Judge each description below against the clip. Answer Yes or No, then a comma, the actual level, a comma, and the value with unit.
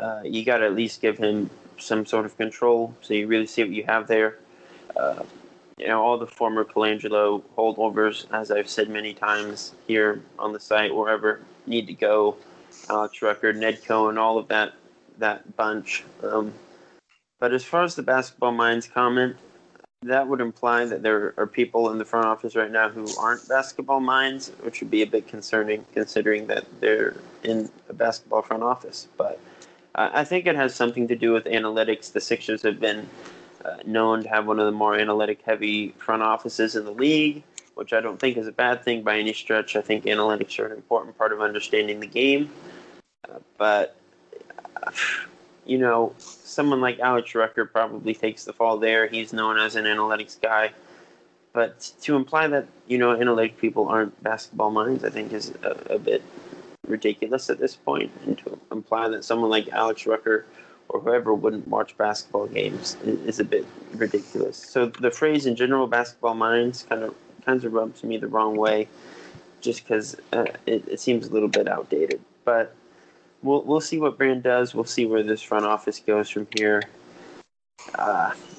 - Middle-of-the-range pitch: No, low, 110 Hz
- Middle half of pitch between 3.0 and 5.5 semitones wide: No, narrow, 2.4 semitones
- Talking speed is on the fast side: No, average, 185 wpm